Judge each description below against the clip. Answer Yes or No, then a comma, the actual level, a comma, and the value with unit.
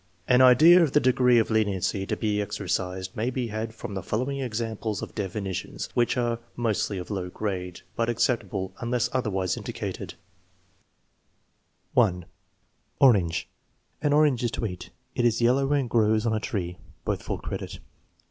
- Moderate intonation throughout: Yes, average, 4.1 semitones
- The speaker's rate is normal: Yes, average, 160 wpm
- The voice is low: Yes, low, 110 Hz